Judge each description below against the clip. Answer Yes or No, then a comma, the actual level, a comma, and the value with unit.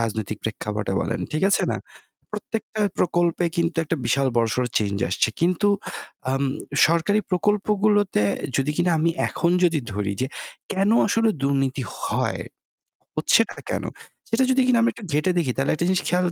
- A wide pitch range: Yes, wide, 7.4 semitones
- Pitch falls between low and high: Yes, medium, 170 Hz